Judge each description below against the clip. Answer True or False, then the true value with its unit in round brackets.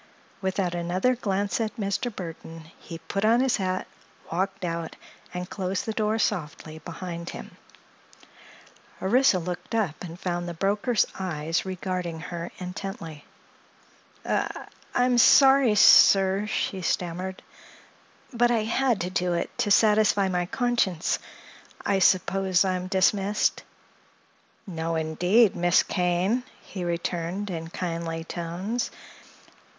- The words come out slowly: True (120 wpm)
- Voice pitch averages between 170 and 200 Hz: True (185 Hz)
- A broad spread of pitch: False (3.2 semitones)